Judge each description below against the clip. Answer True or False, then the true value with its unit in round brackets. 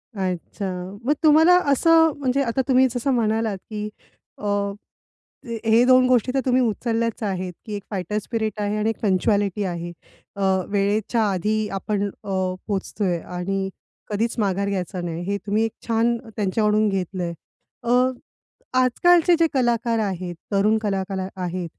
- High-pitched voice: True (210 Hz)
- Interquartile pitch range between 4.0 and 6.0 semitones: False (3.5 semitones)